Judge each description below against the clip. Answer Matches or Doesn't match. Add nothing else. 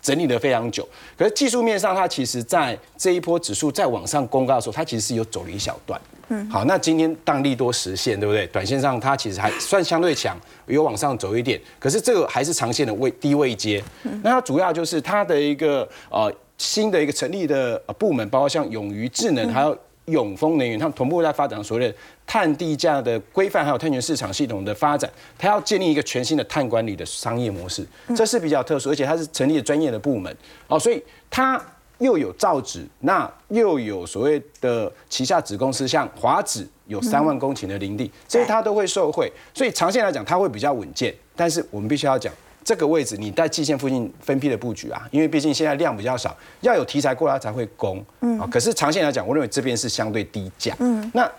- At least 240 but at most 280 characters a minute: Doesn't match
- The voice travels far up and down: Matches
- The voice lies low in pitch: Doesn't match